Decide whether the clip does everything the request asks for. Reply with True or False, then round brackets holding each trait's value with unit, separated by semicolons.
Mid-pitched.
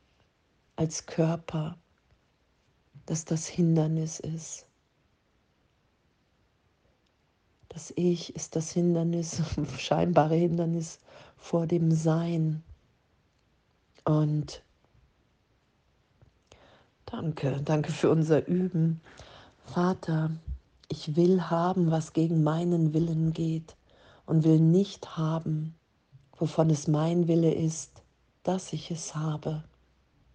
True (160 Hz)